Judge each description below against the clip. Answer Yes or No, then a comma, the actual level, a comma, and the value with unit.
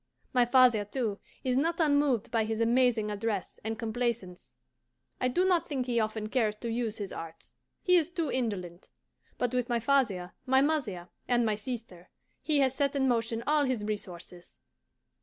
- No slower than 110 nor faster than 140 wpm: No, average, 175 wpm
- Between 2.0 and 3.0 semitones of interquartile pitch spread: No, average, 3.8 semitones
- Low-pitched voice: No, high, 235 Hz